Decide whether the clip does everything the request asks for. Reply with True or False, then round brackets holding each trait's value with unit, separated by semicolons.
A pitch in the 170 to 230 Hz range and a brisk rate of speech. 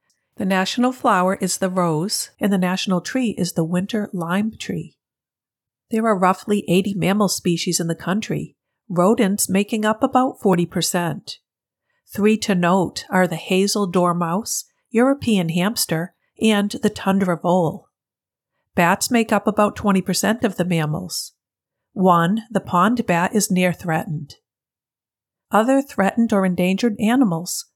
False (190 Hz; 135 wpm)